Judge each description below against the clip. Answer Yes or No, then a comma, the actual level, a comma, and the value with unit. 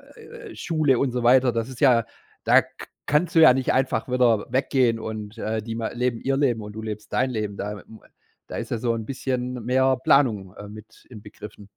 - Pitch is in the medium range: No, low, 120 Hz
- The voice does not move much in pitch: No, average, 3.2 semitones